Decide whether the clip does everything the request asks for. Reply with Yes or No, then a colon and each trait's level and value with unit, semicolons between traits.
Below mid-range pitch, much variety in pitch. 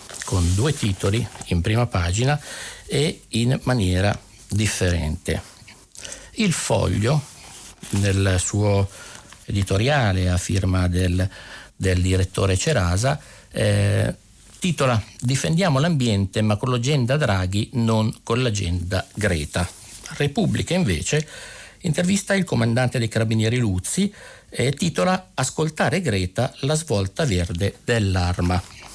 Yes: low, 110 Hz; wide, 5.7 semitones